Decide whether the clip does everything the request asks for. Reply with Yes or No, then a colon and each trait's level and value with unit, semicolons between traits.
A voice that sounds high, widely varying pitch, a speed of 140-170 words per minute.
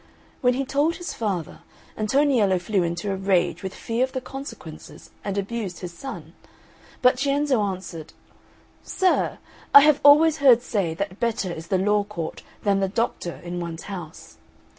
Yes: high, 205 Hz; wide, 6.6 semitones; average, 160 wpm